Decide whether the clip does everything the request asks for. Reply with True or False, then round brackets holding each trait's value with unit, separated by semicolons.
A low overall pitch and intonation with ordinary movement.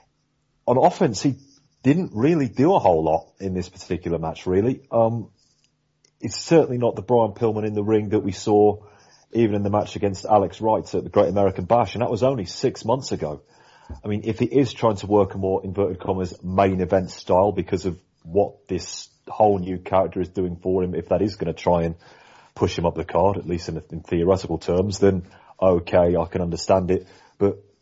True (100 Hz; 3.7 semitones)